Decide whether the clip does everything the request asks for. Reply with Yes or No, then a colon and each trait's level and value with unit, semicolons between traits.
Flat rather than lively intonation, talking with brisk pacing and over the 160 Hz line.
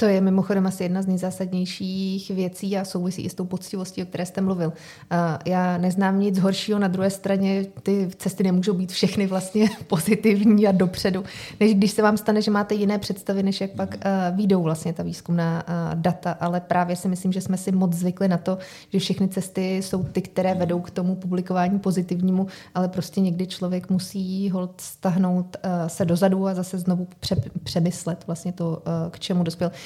Yes: narrow, 1.5 semitones; fast, 185 wpm; medium, 185 Hz